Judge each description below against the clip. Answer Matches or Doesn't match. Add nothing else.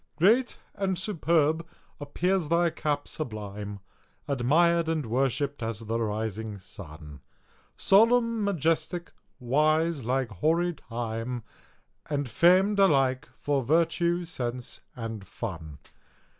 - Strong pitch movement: Matches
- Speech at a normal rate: Doesn't match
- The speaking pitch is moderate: Matches